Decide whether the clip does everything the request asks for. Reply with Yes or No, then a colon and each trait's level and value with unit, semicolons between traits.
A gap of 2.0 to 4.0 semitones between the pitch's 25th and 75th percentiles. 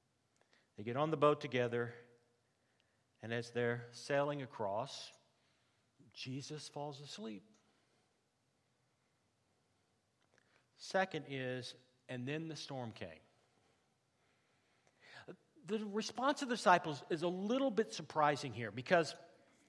No: average, 4.6 semitones